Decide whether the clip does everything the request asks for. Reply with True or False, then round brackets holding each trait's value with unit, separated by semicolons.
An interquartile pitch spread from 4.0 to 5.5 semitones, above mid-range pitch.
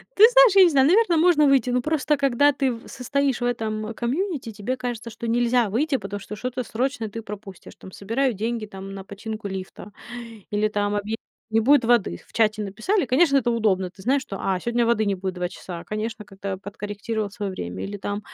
True (4.5 semitones; 225 Hz)